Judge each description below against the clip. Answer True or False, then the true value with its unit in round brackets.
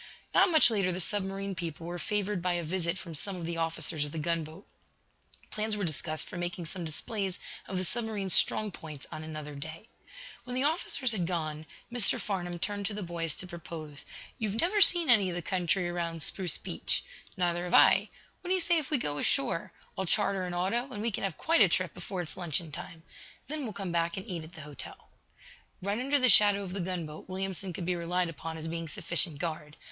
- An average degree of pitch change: True (3.6 semitones)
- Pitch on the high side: False (180 Hz)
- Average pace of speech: False (215 wpm)